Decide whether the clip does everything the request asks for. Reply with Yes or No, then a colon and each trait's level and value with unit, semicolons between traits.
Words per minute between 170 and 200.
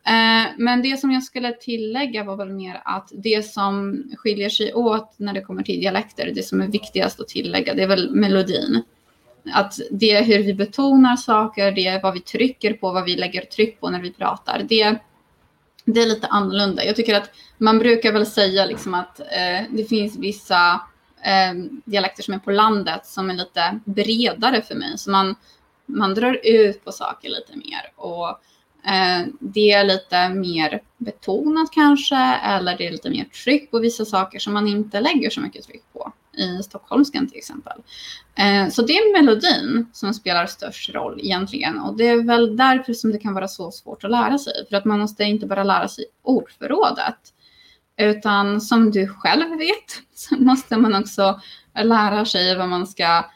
Yes: average, 185 wpm